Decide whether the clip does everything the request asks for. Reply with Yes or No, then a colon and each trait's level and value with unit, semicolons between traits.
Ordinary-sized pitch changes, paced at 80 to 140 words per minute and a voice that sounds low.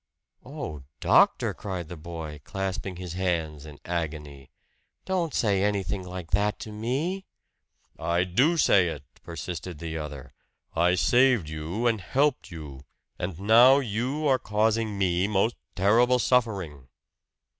No: wide, 5.7 semitones; slow, 135 wpm; very low, 95 Hz